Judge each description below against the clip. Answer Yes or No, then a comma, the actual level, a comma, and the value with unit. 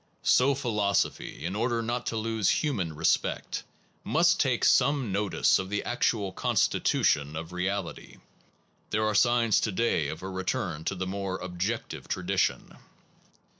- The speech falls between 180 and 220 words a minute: No, average, 140 wpm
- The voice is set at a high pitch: No, low, 100 Hz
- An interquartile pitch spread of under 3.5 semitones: No, average, 4.0 semitones